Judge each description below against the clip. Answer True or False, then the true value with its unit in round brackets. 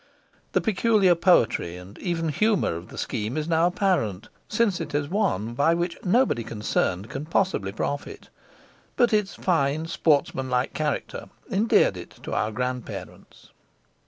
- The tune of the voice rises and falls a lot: True (8.0 semitones)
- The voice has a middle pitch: True (155 Hz)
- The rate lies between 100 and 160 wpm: True (140 wpm)